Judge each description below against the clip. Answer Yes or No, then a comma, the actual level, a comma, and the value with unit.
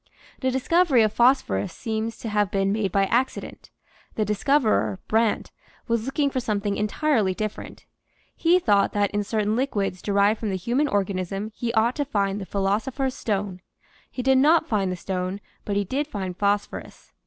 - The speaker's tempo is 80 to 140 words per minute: No, average, 170 wpm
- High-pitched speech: Yes, high, 210 Hz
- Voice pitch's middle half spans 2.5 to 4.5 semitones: Yes, average, 4.2 semitones